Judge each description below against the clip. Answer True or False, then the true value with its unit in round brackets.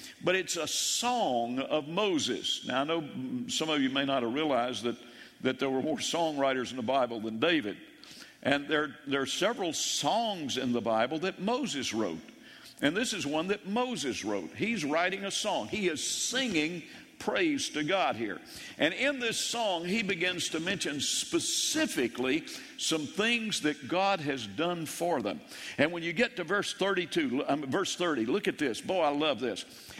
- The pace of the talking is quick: False (180 wpm)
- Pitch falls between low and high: True (170 Hz)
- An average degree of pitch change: False (8.7 semitones)